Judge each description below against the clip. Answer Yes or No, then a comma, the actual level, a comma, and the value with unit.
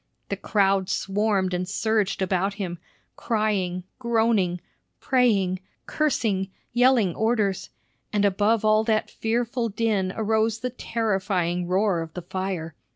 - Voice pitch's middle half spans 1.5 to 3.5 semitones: Yes, average, 3.0 semitones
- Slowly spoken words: Yes, slow, 120 wpm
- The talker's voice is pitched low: No, high, 205 Hz